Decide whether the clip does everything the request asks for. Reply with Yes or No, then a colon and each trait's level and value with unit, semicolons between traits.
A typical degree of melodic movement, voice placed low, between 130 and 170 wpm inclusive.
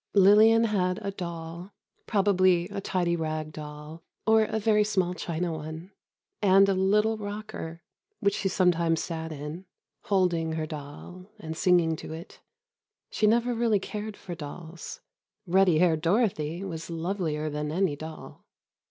No: average, 3.9 semitones; medium, 180 Hz; average, 145 wpm